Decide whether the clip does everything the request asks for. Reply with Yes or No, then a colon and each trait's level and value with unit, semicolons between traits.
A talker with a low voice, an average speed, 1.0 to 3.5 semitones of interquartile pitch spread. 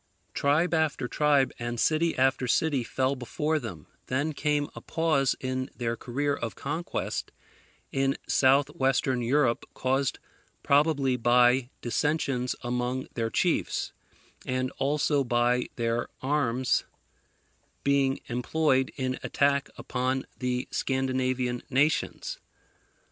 No: low, 130 Hz; slow, 110 wpm; narrow, 2.4 semitones